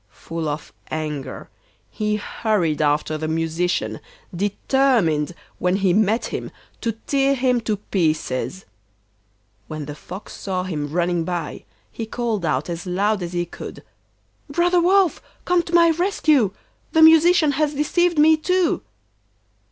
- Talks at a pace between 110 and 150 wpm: Yes, slow, 135 wpm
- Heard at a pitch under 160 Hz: No, high, 205 Hz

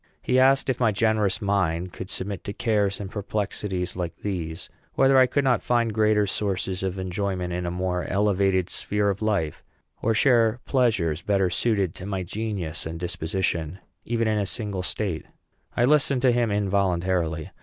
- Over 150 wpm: Yes, average, 170 wpm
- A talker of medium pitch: No, low, 100 Hz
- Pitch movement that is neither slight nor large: Yes, average, 3.4 semitones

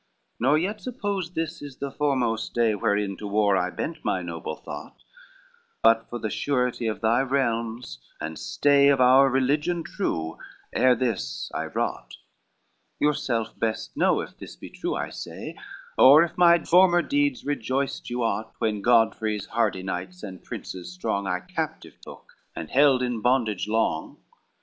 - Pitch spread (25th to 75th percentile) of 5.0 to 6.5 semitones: Yes, average, 5.3 semitones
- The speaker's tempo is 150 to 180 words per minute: Yes, average, 160 wpm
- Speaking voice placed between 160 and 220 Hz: No, low, 120 Hz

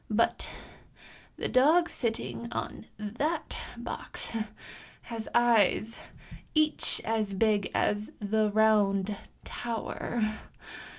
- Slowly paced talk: Yes, slow, 85 wpm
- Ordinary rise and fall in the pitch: No, narrow, 2.2 semitones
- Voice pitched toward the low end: No, high, 220 Hz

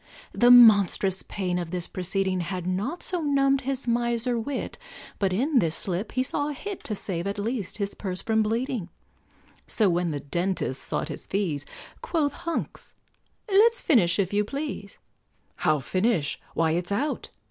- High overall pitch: Yes, high, 205 Hz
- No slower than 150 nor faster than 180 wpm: Yes, average, 165 wpm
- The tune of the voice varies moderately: No, wide, 6.2 semitones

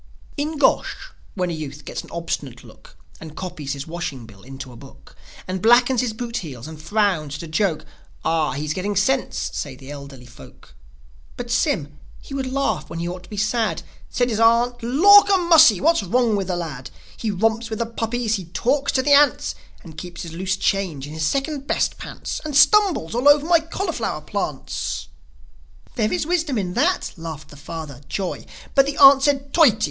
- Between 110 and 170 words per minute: No, average, 195 wpm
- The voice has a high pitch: Yes, high, 205 Hz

